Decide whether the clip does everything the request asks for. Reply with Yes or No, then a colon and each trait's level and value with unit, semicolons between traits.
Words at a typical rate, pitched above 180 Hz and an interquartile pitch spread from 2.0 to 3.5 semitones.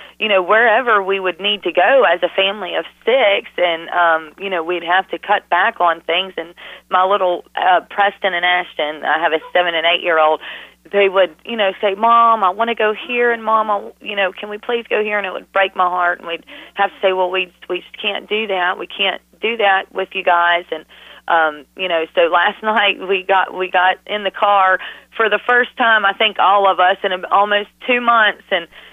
No: fast, 230 wpm; high, 190 Hz; average, 2.7 semitones